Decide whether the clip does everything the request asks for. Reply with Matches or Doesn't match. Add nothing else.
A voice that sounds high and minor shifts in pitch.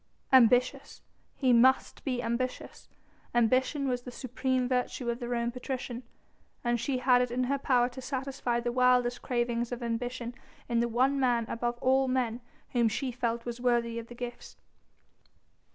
Matches